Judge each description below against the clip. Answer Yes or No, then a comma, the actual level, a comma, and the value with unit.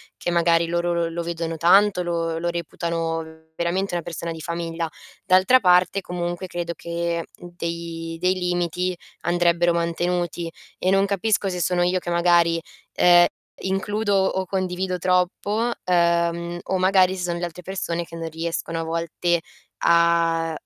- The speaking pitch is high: No, medium, 175 Hz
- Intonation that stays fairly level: Yes, narrow, 1.4 semitones